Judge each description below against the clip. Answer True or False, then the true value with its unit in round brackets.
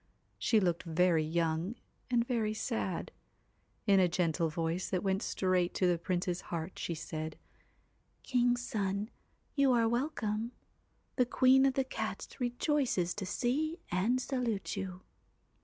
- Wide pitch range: True (5.7 semitones)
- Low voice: False (200 Hz)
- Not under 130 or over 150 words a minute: True (140 wpm)